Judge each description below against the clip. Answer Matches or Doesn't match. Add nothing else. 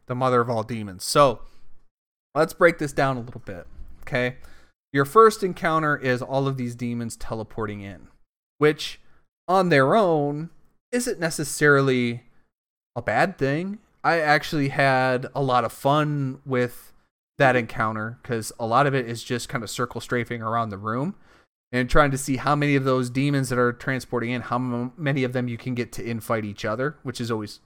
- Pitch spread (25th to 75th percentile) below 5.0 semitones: Matches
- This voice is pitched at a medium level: Doesn't match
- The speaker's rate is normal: Matches